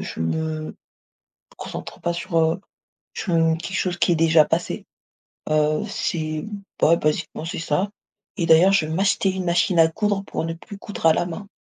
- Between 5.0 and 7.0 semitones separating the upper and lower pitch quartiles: No, average, 2.7 semitones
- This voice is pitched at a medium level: Yes, medium, 165 Hz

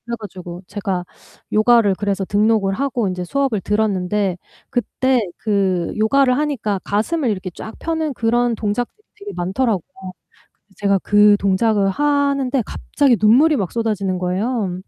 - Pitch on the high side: Yes, high, 215 Hz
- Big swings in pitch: No, average, 4.4 semitones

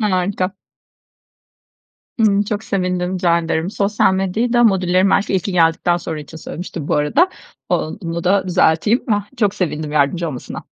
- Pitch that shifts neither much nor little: Yes, average, 3.2 semitones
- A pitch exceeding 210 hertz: No, medium, 185 Hz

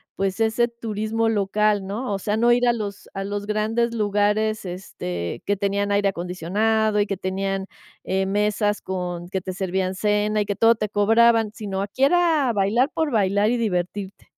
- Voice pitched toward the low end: No, high, 205 Hz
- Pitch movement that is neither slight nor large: No, narrow, 2.3 semitones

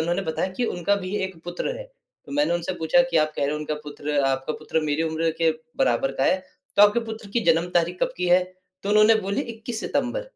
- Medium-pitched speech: Yes, medium, 180 Hz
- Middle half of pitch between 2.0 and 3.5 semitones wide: No, average, 4.8 semitones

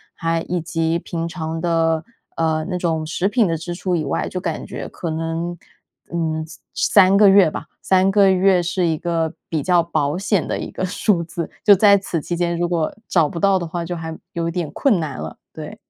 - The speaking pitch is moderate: Yes, medium, 170 Hz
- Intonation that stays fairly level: Yes, narrow, 2.1 semitones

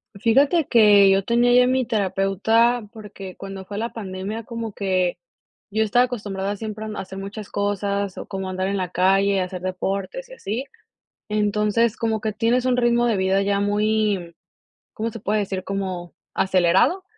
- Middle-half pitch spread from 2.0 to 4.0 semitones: Yes, average, 2.9 semitones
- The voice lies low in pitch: No, high, 205 Hz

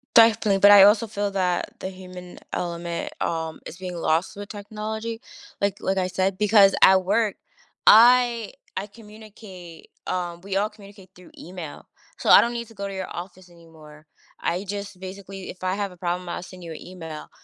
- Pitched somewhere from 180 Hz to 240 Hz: Yes, high, 190 Hz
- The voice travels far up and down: No, narrow, 2.6 semitones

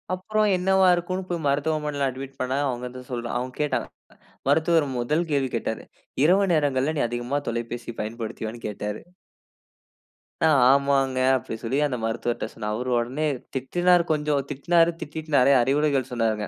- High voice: No, low, 135 Hz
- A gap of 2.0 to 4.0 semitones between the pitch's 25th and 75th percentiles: No, average, 4.4 semitones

